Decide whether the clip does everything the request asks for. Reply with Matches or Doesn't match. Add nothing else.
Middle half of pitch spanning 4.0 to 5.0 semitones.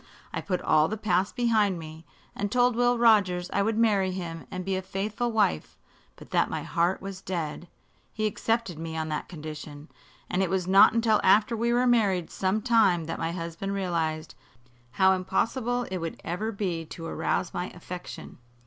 Matches